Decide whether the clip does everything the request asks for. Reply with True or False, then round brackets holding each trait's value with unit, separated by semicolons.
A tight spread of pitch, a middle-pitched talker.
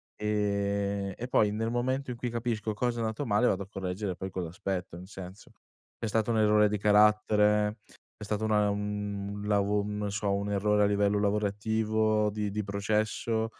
False (1.3 semitones; 105 Hz)